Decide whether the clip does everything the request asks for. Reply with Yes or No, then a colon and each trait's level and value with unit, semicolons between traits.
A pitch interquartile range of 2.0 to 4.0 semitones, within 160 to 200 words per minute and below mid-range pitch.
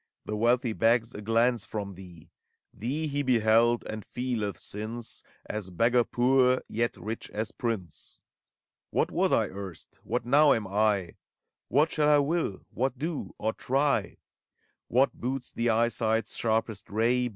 No: average, 2.8 semitones; average, 150 wpm; low, 115 Hz